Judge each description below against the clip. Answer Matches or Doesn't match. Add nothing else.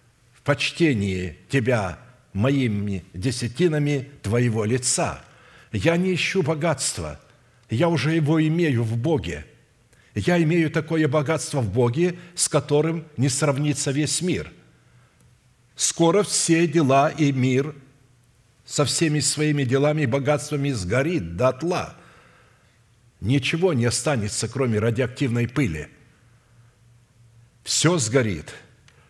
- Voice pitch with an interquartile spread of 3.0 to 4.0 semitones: Doesn't match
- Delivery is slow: Matches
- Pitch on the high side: Doesn't match